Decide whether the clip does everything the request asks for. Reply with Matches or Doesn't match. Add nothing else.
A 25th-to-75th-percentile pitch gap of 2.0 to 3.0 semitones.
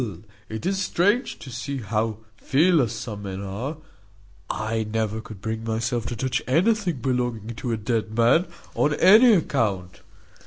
Doesn't match